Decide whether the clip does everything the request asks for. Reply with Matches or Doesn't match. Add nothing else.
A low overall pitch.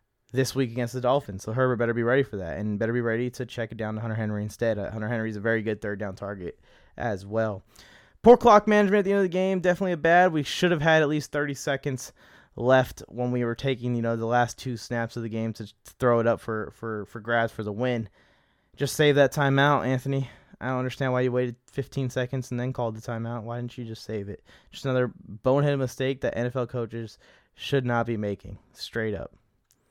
Matches